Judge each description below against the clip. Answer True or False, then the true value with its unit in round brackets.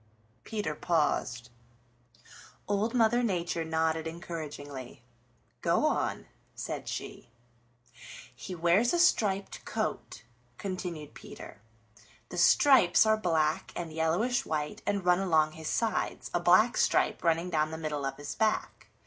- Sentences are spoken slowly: True (125 wpm)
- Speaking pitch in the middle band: True (170 Hz)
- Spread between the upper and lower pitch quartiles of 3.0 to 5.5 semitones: True (4.6 semitones)